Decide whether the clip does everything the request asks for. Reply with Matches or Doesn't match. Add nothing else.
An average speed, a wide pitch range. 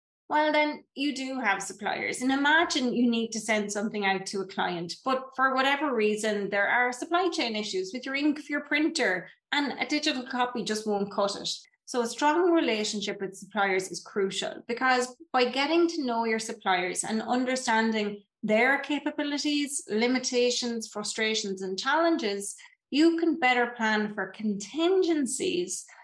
Matches